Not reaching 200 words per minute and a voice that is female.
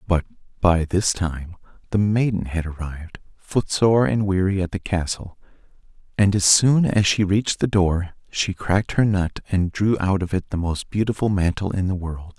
No: average, 185 wpm; male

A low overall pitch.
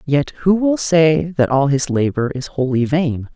No: medium, 145 Hz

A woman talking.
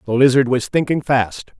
No: male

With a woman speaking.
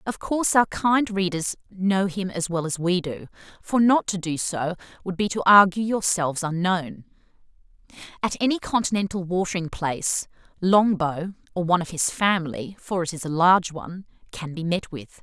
Yes: female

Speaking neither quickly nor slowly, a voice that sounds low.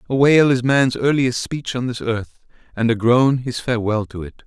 No: fast, 215 wpm; low, 120 Hz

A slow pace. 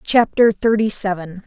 Yes: slow, 125 wpm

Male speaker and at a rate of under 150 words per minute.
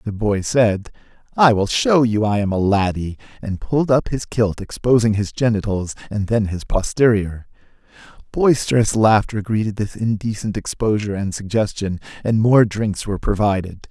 No: male; average, 155 wpm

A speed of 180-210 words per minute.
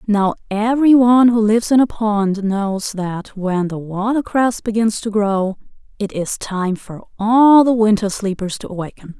No: average, 170 wpm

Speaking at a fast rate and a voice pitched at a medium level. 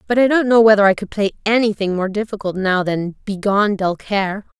No: fast, 210 wpm; high, 205 Hz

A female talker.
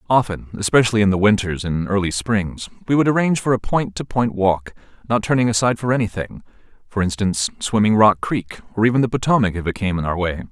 No: male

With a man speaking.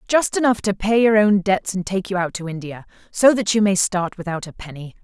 No: female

